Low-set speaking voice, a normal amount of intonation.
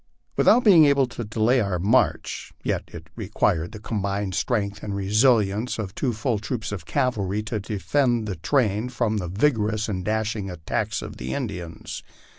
Yes: low, 105 Hz; average, 3.6 semitones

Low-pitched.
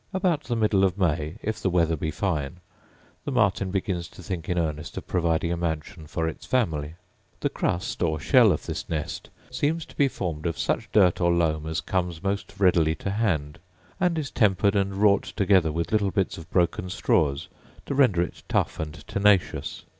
Yes: very low, 90 Hz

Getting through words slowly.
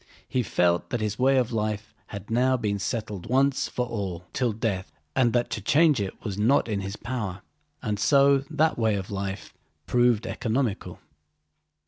No: average, 170 wpm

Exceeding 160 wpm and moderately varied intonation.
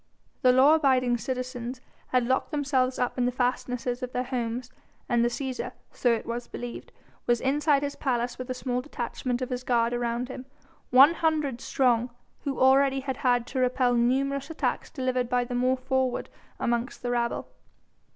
No: average, 175 wpm; narrow, 1.5 semitones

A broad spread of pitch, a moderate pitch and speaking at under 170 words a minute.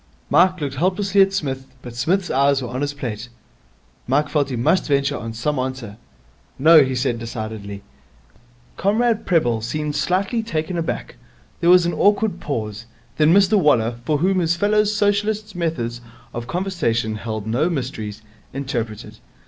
Yes: wide, 7.4 semitones; medium, 145 Hz; average, 155 wpm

